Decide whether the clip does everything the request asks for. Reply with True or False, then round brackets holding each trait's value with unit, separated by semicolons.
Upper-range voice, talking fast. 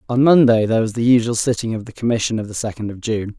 False (115 Hz; 265 wpm)